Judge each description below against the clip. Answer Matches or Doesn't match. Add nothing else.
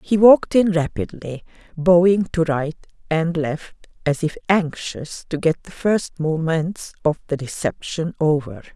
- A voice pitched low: Doesn't match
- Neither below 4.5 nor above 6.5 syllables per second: Doesn't match